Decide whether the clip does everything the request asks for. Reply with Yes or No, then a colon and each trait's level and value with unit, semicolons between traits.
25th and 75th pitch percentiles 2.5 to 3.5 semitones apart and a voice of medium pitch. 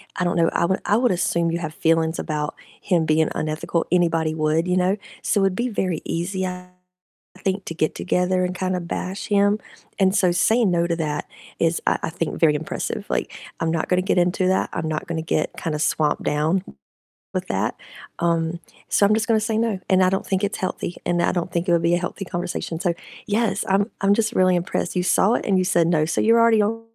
Yes: average, 2.8 semitones; medium, 180 Hz